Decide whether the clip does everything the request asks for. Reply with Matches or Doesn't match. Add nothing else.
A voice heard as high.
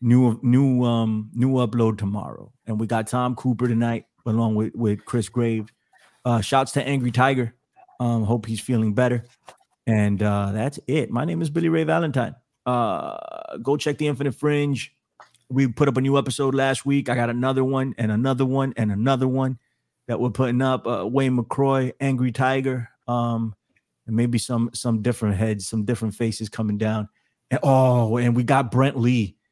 Doesn't match